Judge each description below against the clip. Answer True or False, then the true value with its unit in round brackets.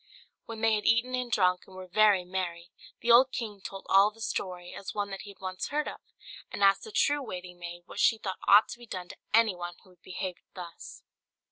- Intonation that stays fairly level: False (3.6 semitones)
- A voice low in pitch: False (195 Hz)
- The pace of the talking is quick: True (230 wpm)